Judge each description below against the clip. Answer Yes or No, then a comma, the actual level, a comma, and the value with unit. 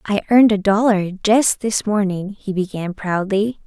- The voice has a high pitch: Yes, high, 205 Hz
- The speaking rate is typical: Yes, average, 165 wpm